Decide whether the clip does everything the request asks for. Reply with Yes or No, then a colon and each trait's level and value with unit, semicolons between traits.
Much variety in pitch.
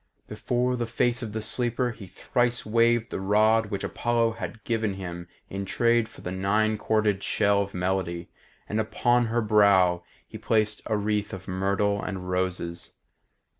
No: average, 3.2 semitones